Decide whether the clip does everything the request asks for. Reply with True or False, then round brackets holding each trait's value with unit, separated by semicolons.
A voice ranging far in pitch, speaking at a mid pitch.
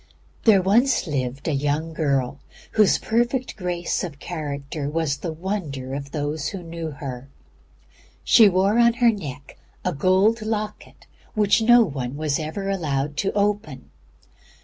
True (6.4 semitones; 165 Hz)